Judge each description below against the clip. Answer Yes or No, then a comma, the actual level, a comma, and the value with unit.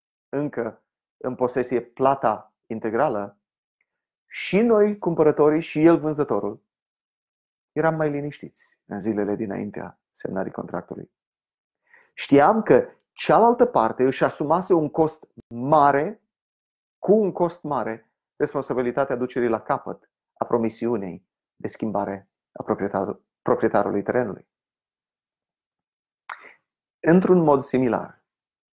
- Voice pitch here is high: No, medium, 140 Hz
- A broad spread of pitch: Yes, wide, 5.8 semitones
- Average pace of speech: No, slow, 100 wpm